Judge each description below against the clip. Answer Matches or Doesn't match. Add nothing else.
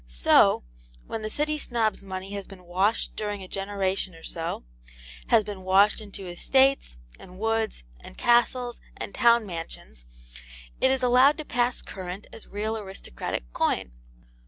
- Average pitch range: Matches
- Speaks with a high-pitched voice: Matches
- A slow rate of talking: Doesn't match